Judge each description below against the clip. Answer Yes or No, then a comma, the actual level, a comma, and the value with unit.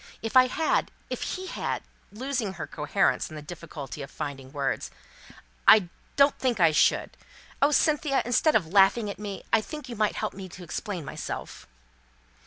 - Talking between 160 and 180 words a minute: Yes, average, 175 wpm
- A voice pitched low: No, high, 205 Hz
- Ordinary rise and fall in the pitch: No, wide, 7.5 semitones